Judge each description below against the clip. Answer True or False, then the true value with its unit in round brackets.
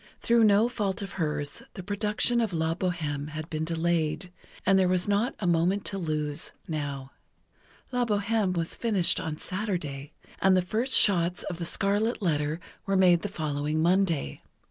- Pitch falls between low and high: True (180 Hz)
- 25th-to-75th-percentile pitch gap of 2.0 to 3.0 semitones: False (4.4 semitones)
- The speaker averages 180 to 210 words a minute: False (165 wpm)